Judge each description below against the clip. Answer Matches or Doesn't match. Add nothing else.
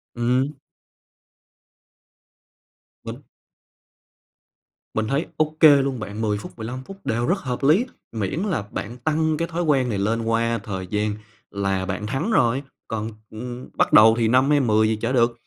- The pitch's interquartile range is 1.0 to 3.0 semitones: Doesn't match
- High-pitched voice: Doesn't match